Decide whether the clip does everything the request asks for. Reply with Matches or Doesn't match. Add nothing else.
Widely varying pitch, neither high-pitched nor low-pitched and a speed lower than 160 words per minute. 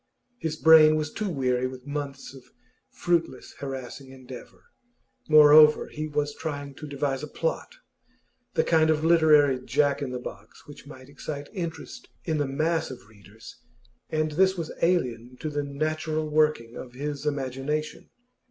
Doesn't match